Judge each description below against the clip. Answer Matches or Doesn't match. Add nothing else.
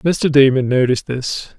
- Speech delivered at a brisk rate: Doesn't match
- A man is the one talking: Matches